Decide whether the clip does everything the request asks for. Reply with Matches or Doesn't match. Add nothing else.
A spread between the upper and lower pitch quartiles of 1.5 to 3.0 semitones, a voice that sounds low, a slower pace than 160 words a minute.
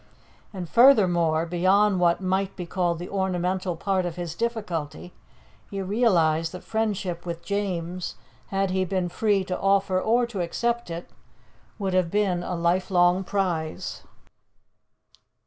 Doesn't match